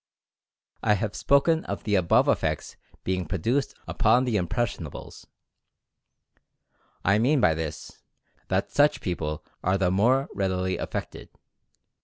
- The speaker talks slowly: Yes, slow, 120 wpm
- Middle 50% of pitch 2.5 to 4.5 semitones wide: No, average, 5.2 semitones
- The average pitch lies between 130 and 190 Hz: No, low, 100 Hz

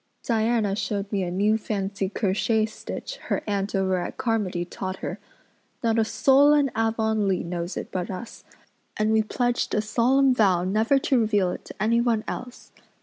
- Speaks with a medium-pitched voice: No, high, 215 Hz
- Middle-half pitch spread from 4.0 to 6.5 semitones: No, average, 3.1 semitones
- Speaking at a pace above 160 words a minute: Yes, average, 170 wpm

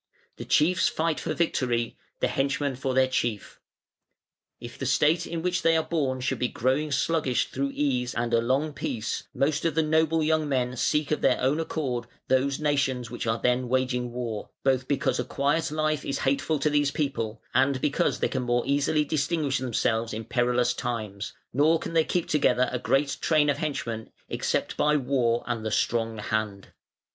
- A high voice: No, low, 135 Hz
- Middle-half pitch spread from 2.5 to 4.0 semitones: Yes, average, 3.7 semitones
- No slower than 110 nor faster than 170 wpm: No, average, 185 wpm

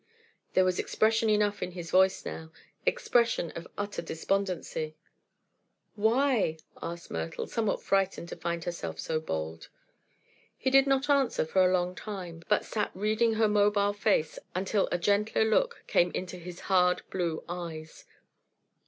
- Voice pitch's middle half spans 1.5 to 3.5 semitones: No, average, 4.0 semitones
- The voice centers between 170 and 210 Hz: Yes, high, 190 Hz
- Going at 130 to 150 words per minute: Yes, average, 145 wpm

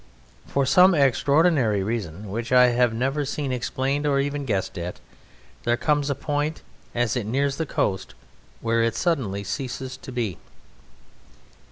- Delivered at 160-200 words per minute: No, average, 150 wpm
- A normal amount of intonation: Yes, average, 3.9 semitones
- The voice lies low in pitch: Yes, low, 130 Hz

